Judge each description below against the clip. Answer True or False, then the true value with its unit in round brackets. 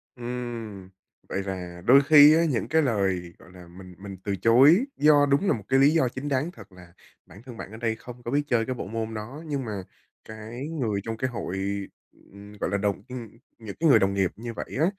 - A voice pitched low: True (115 Hz)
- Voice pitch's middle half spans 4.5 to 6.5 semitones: True (5.5 semitones)